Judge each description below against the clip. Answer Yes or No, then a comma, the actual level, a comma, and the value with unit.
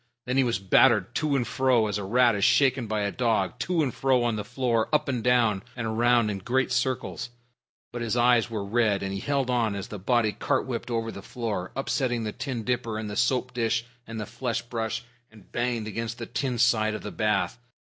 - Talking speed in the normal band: No, fast, 225 wpm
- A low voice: Yes, low, 115 Hz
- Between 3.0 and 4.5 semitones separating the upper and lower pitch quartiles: No, narrow, 2.4 semitones